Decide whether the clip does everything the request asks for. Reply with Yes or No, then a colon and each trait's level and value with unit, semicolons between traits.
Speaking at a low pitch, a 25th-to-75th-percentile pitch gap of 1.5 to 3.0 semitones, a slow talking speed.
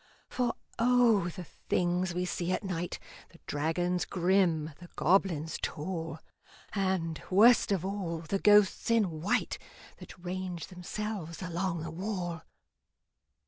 No: medium, 180 Hz; average, 2.7 semitones; slow, 125 wpm